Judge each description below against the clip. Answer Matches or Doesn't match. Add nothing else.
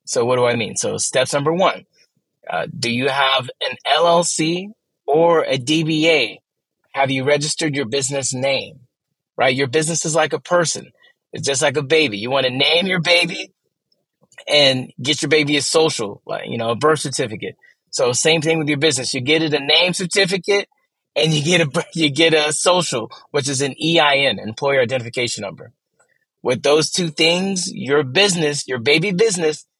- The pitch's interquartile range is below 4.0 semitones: Matches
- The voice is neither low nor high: Matches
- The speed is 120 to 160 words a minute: Doesn't match